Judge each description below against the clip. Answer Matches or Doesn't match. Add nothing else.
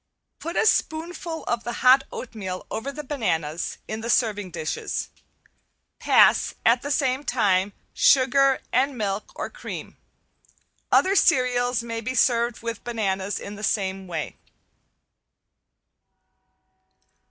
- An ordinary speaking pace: Doesn't match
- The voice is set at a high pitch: Matches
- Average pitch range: Matches